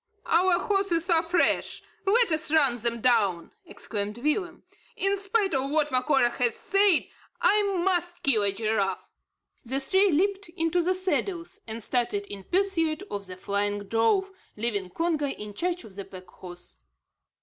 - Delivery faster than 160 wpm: No, average, 155 wpm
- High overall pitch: Yes, very high, 295 Hz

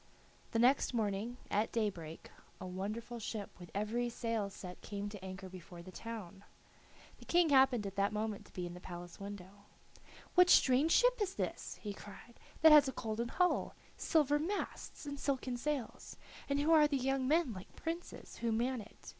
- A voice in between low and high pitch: No, high, 230 Hz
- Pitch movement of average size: No, wide, 5.7 semitones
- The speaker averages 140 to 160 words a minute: No, average, 180 wpm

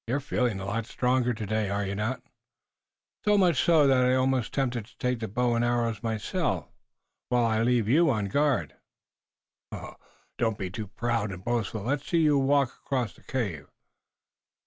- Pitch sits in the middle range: No, low, 120 Hz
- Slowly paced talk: No, average, 175 wpm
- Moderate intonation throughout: Yes, average, 3.5 semitones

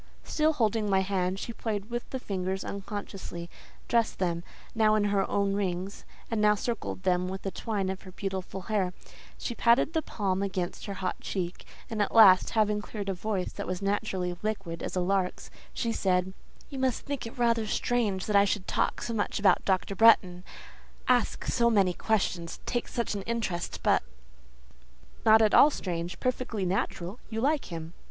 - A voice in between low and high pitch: No, high, 200 Hz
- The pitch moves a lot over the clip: No, average, 3.3 semitones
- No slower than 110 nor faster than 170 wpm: No, average, 180 wpm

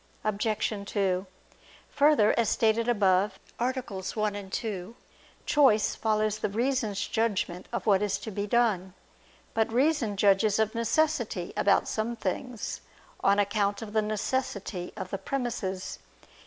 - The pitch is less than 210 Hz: No, high, 215 Hz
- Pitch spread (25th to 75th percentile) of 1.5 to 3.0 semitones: Yes, average, 2.7 semitones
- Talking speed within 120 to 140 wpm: Yes, slow, 135 wpm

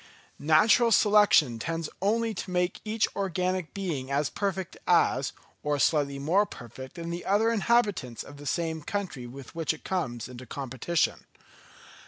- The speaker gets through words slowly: No, average, 150 wpm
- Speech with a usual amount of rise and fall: No, wide, 6.1 semitones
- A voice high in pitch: No, medium, 170 Hz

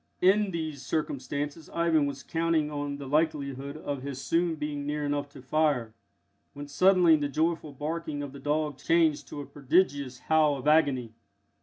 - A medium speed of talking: Yes, average, 165 wpm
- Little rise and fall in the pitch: Yes, narrow, 2.2 semitones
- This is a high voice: No, medium, 145 Hz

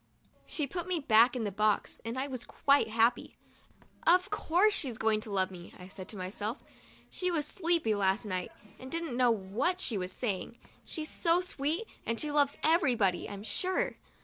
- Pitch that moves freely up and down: Yes, wide, 7.5 semitones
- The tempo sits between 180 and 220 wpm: Yes, average, 185 wpm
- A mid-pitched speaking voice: No, high, 245 Hz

